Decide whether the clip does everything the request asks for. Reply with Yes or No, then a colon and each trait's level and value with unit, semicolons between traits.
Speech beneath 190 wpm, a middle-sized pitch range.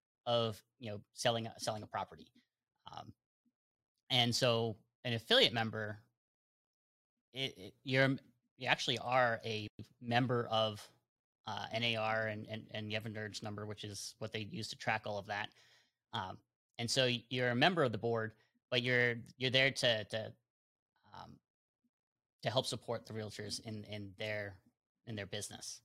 No: average, 165 wpm; narrow, 2.2 semitones